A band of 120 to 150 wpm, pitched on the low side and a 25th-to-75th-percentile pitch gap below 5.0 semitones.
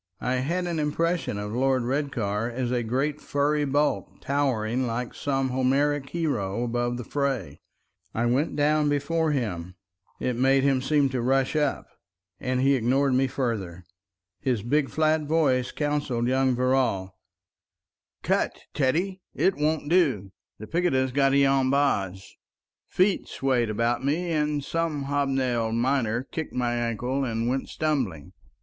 Yes: average, 140 wpm; low, 130 Hz; average, 3.5 semitones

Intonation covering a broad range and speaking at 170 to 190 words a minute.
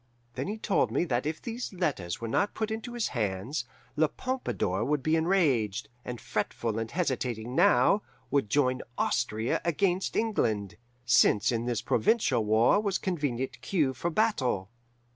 No: wide, 8.5 semitones; average, 155 wpm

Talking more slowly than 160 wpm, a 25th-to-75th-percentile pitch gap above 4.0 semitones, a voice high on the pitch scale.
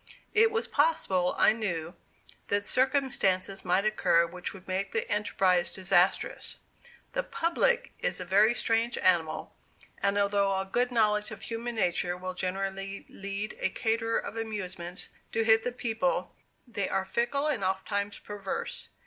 No: average, 150 wpm; average, 3.5 semitones; high, 205 Hz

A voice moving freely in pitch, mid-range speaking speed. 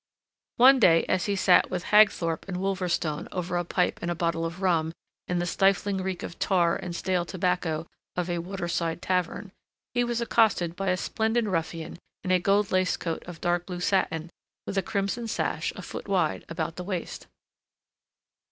No: narrow, 2.4 semitones; average, 180 wpm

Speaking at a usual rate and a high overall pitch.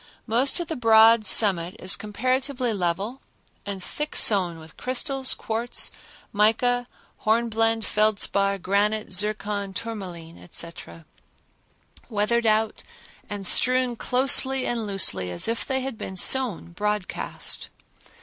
No: slow, 115 wpm; high, 215 Hz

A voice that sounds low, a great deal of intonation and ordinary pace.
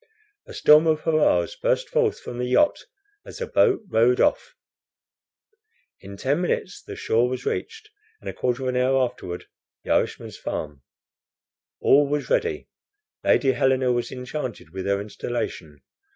Yes: low, 130 Hz; wide, 7.2 semitones; average, 150 wpm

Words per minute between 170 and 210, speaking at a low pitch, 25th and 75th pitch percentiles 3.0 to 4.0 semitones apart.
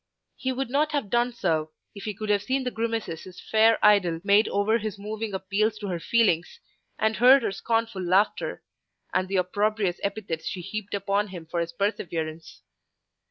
No: average, 180 wpm; high, 205 Hz; average, 3.4 semitones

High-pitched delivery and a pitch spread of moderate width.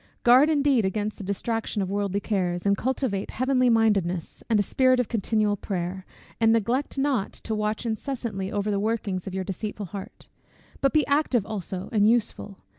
Yes: high, 215 Hz; average, 3.6 semitones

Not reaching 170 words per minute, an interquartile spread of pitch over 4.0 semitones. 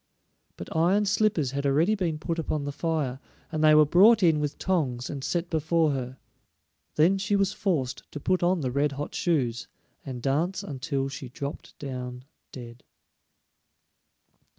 Yes: average, 160 wpm; average, 4.5 semitones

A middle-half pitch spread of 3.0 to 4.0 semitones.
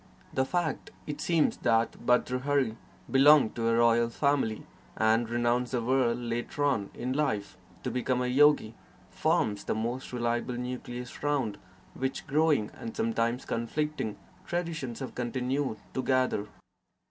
Yes: average, 3.4 semitones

